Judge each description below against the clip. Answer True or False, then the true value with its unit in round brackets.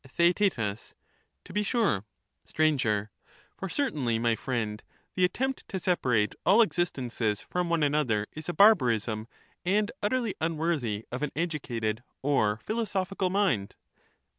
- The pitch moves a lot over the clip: True (9.0 semitones)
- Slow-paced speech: True (130 wpm)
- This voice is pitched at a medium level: True (150 Hz)